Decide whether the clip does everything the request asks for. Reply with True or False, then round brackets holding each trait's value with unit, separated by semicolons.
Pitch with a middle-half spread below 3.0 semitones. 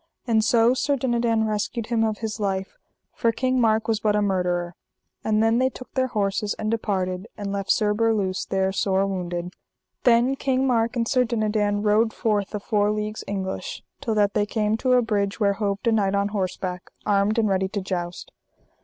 True (2.5 semitones)